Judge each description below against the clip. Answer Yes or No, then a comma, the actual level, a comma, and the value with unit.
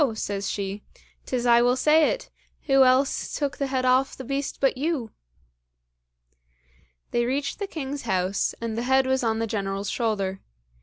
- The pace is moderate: Yes, average, 165 wpm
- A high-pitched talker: Yes, very high, 255 Hz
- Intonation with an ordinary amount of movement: Yes, average, 3.8 semitones